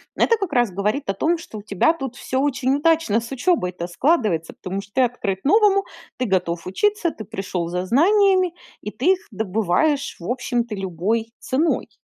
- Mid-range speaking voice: No, high, 245 Hz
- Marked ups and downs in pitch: Yes, wide, 8.8 semitones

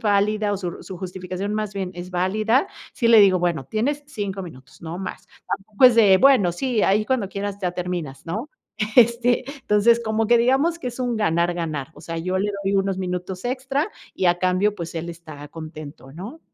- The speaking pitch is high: Yes, high, 195 Hz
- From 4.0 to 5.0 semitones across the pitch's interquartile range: Yes, average, 4.6 semitones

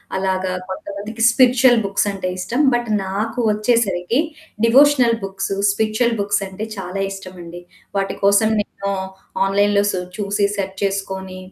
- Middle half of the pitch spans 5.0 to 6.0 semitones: No, average, 2.9 semitones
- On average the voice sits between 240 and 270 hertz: No, high, 200 Hz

